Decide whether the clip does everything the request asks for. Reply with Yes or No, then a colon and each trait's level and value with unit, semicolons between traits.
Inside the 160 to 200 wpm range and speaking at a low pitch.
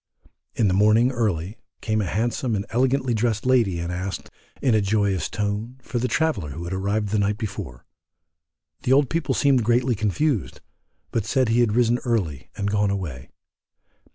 Yes: average, 175 wpm; low, 110 Hz